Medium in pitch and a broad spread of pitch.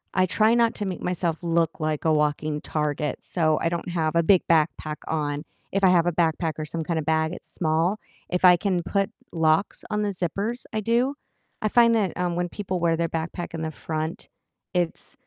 No: medium, 170 Hz; average, 3.0 semitones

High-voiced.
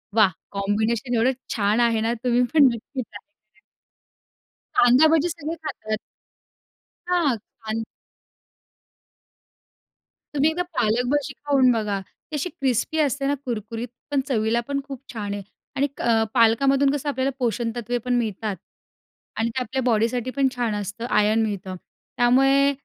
Yes: high, 245 Hz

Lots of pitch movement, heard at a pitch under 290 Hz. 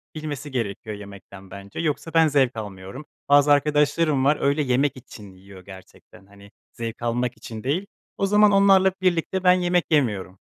Yes: wide, 7.6 semitones; low, 135 Hz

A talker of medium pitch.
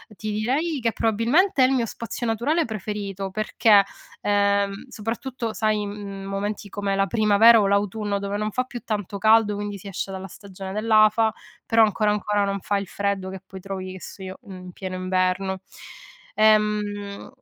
No: high, 205 Hz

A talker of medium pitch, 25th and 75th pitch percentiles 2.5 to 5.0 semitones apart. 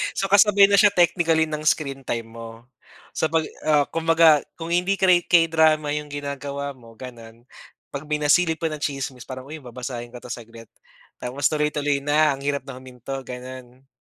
Yes: medium, 145 Hz; average, 3.9 semitones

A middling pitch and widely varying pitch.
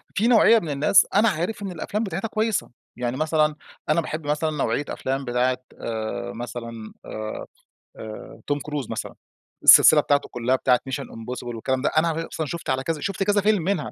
Yes: medium, 150 Hz; wide, 5.8 semitones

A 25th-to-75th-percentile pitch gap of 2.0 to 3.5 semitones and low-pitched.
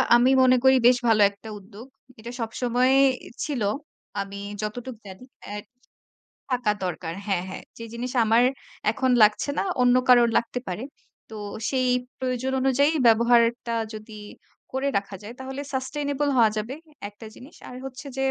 No: average, 3.2 semitones; high, 240 Hz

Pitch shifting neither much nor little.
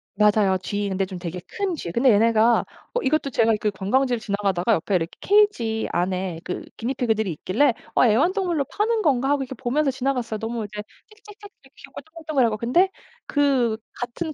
No: wide, 5.8 semitones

